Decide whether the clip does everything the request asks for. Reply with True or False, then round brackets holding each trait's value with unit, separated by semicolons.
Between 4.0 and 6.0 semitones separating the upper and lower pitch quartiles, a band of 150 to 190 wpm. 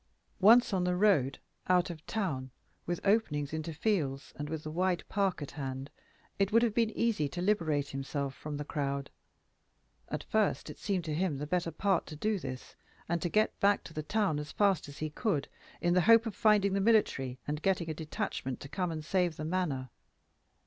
False (5.2 semitones; 205 wpm)